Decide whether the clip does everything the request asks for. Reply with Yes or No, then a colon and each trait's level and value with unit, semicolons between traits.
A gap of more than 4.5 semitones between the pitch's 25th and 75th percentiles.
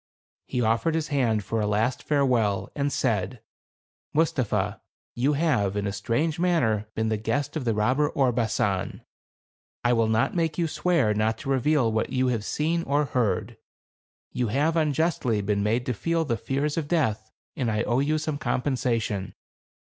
Yes: average, 5.3 semitones